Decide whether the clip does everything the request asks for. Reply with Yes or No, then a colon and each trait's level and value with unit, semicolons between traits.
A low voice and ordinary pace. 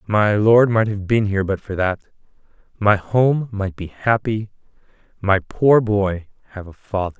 Yes: low, 105 Hz; average, 165 wpm